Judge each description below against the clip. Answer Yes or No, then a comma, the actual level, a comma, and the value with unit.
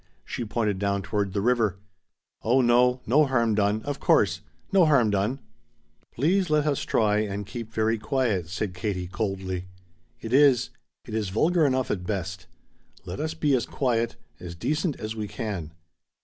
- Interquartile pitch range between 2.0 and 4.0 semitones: No, average, 4.8 semitones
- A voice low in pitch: Yes, low, 110 Hz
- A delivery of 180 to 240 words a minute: No, average, 170 wpm